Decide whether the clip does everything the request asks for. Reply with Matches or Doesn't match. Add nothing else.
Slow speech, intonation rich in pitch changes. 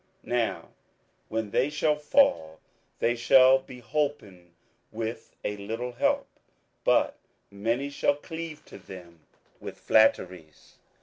Matches